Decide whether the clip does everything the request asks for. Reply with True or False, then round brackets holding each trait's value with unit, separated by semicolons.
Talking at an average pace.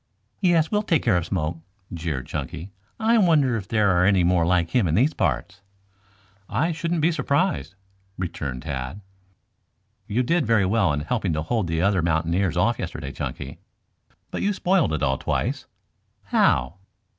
True (165 wpm)